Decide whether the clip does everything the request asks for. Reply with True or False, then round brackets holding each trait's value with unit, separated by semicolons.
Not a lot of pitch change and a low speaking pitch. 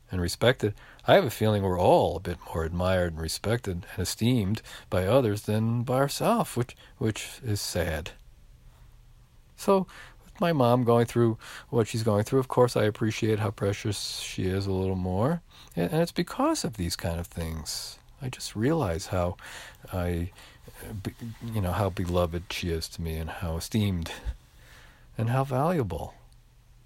False (5.1 semitones; 110 Hz)